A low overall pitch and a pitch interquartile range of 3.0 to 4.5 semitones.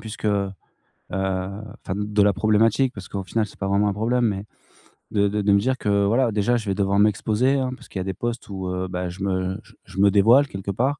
No: low, 100 Hz; narrow, 2.5 semitones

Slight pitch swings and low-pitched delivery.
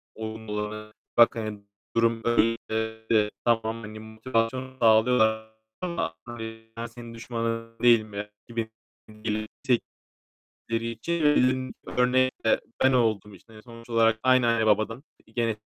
Yes: narrow, 1.5 semitones; low, 115 Hz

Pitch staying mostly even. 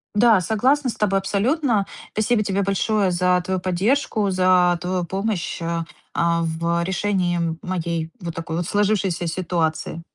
No: average, 3.4 semitones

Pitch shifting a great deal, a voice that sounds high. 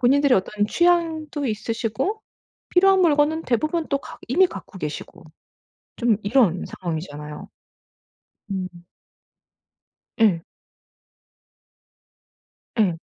Yes: wide, 8.9 semitones; high, 240 Hz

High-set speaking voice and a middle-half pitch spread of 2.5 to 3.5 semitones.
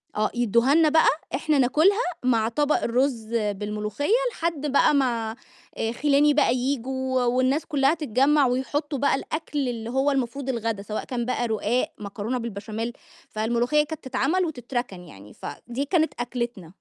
No: very high, 255 Hz; average, 4.0 semitones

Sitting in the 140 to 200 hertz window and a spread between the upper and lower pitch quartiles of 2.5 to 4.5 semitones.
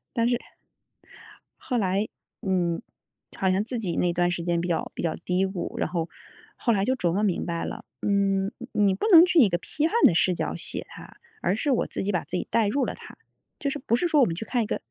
No: high, 195 Hz; average, 5.2 semitones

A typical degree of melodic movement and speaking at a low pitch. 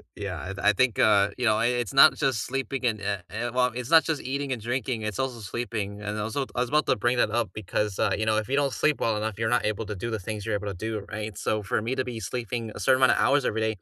Yes: average, 3.1 semitones; low, 110 Hz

